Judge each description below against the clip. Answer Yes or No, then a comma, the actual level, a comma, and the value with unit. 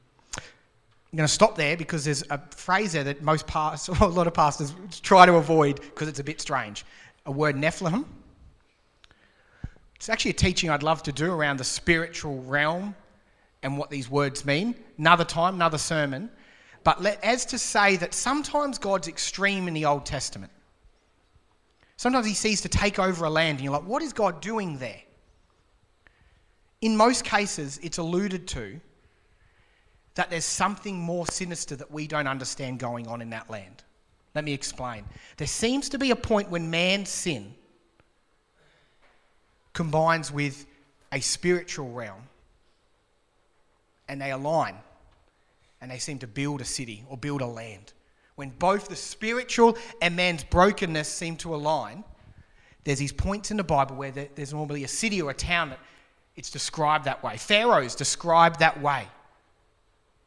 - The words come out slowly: No, average, 160 wpm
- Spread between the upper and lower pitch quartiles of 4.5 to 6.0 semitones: Yes, wide, 5.5 semitones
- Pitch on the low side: No, medium, 150 Hz